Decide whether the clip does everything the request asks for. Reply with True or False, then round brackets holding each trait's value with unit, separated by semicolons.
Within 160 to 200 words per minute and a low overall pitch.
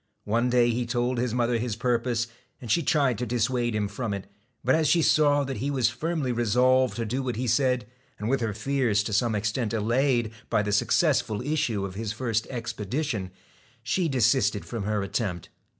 True (195 wpm; 120 Hz)